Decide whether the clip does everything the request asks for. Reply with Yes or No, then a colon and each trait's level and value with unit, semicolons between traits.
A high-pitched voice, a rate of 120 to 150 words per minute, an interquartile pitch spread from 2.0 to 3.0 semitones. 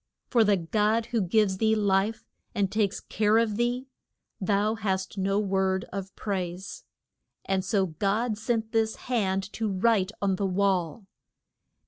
Yes: high, 200 Hz; average, 145 wpm; narrow, 2.5 semitones